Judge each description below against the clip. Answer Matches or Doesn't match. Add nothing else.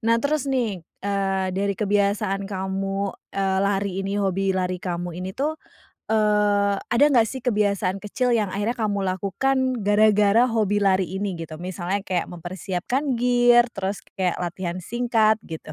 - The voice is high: Matches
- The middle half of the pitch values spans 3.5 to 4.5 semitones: Doesn't match